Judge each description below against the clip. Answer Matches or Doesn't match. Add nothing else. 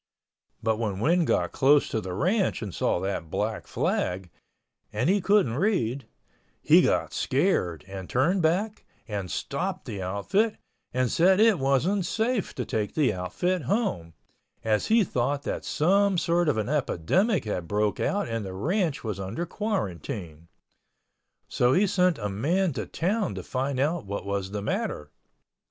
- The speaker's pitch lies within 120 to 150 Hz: Matches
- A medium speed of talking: Matches